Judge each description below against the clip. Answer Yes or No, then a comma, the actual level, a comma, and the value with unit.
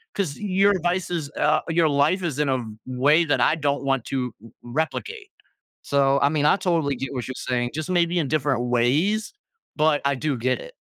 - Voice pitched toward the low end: No, medium, 145 Hz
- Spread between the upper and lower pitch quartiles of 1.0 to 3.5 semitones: No, average, 4.5 semitones